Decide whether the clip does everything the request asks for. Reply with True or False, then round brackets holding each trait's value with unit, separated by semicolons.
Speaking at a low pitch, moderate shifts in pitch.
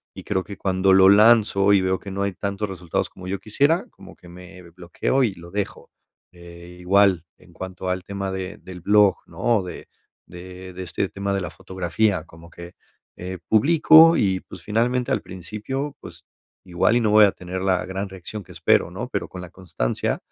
False (95 Hz; 2.3 semitones)